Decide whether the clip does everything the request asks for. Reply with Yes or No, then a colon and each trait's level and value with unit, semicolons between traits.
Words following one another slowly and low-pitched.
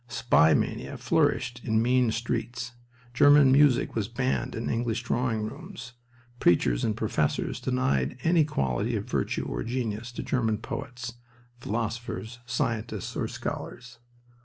Yes: slow, 130 wpm; low, 120 Hz